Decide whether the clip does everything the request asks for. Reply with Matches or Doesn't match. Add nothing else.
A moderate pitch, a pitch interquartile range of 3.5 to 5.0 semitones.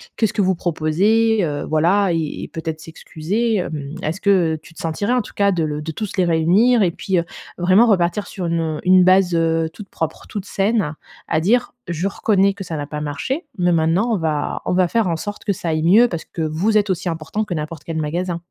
Matches